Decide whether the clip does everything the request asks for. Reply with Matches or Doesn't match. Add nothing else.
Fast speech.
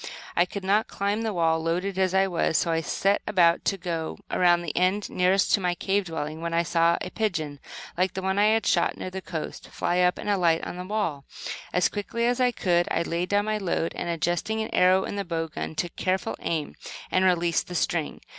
Matches